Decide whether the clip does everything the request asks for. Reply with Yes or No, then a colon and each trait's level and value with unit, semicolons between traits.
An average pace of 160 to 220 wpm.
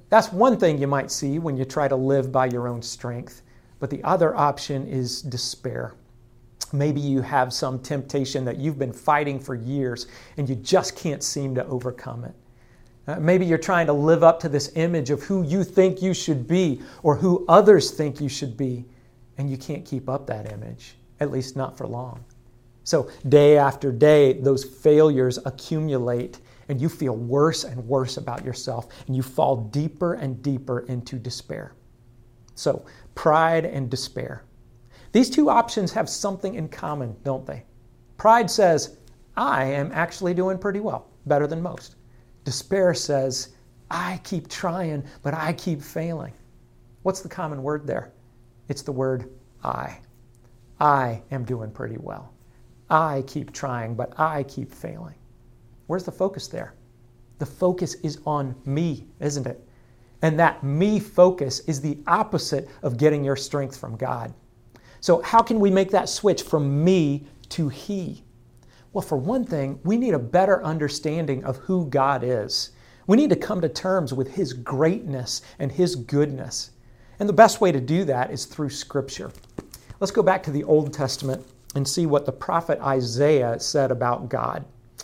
Yes: average, 170 wpm